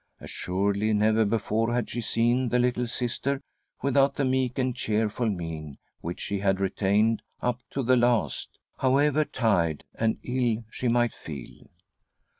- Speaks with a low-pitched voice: Yes, low, 115 Hz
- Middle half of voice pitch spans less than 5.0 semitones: Yes, average, 3.5 semitones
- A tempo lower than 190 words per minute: Yes, average, 145 wpm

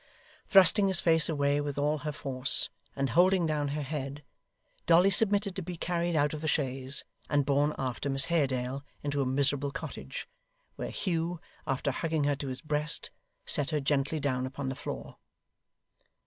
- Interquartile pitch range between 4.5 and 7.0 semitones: No, average, 3.1 semitones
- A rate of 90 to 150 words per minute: No, average, 170 wpm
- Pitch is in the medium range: Yes, medium, 145 Hz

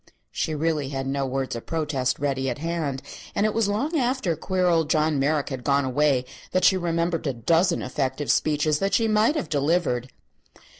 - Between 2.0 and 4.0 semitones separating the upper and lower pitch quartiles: No, average, 4.5 semitones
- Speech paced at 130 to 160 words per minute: No, average, 190 wpm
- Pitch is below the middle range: No, medium, 150 Hz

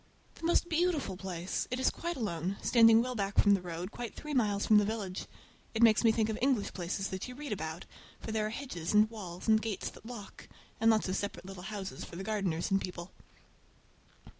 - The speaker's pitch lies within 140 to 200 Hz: No, high, 210 Hz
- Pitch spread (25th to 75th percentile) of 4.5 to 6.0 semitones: No, average, 3.5 semitones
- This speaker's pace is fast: Yes, fast, 215 wpm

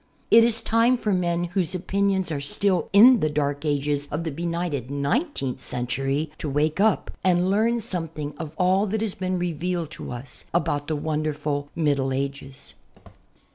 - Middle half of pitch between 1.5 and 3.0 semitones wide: No, average, 4.7 semitones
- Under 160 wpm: No, average, 165 wpm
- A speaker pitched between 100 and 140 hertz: No, medium, 165 Hz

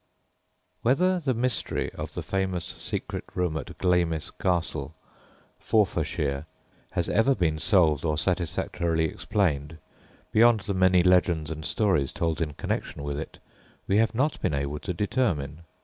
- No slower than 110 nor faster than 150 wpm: Yes, average, 140 wpm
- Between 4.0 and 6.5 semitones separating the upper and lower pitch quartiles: Yes, average, 4.9 semitones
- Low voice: Yes, very low, 90 Hz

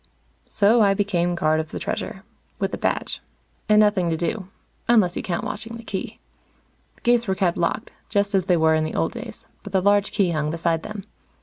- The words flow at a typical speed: No, fast, 210 wpm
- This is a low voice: No, high, 190 Hz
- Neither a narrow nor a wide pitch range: Yes, average, 3.5 semitones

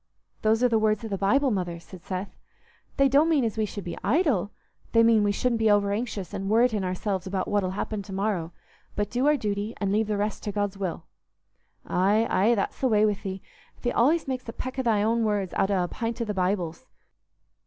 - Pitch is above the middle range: Yes, high, 210 Hz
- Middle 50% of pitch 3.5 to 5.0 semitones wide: No, average, 2.9 semitones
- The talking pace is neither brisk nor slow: No, fast, 225 wpm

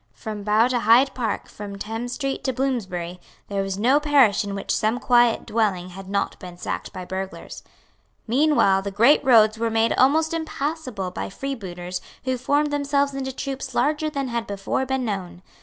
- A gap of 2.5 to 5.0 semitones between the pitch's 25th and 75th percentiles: No, wide, 5.4 semitones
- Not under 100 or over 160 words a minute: No, average, 175 wpm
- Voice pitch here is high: Yes, high, 230 Hz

